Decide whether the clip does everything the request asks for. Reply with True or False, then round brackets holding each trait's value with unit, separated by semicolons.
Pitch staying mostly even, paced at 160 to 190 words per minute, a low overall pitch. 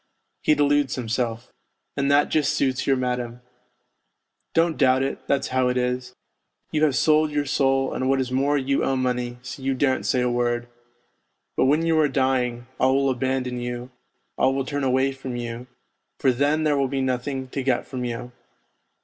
True (2.0 semitones; 185 wpm; 130 Hz)